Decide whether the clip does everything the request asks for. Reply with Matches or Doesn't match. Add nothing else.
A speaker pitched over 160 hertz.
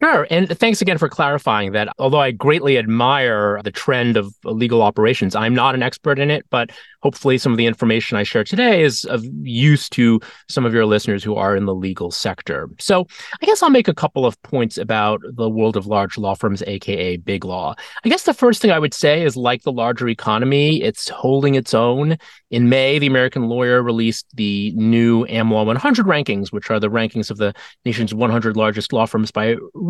Doesn't match